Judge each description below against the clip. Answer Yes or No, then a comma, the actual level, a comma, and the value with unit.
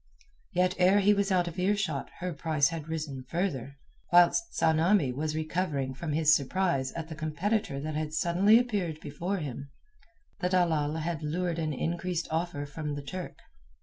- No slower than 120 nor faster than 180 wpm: Yes, average, 165 wpm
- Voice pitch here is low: No, medium, 160 Hz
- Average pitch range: Yes, average, 3.4 semitones